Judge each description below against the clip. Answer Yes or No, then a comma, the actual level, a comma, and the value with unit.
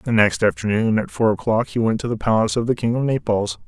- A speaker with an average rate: No, fast, 260 wpm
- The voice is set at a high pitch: No, low, 110 Hz